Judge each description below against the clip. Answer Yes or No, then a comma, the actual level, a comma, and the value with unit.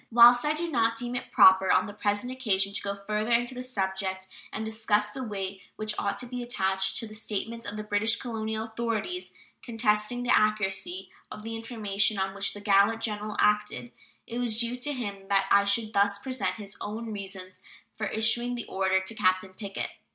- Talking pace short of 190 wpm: No, average, 195 wpm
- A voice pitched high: Yes, high, 215 Hz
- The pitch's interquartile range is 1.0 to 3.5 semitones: Yes, average, 2.8 semitones